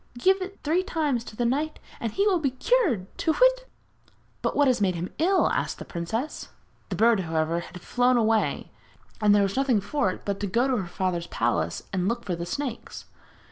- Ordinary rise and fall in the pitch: No, wide, 7.8 semitones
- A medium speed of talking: No, fast, 210 wpm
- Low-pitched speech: No, high, 235 Hz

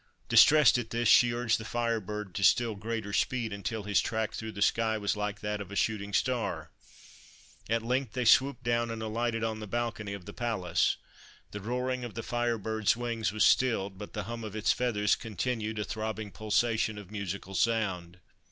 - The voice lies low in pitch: Yes, low, 110 Hz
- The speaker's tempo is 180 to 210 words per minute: Yes, average, 195 wpm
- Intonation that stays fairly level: Yes, narrow, 2.3 semitones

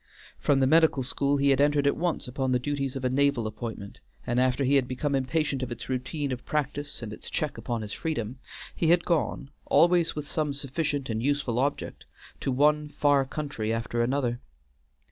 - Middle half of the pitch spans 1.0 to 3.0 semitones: Yes, average, 2.7 semitones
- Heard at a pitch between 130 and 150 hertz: Yes, medium, 140 Hz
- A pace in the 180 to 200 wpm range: Yes, average, 195 wpm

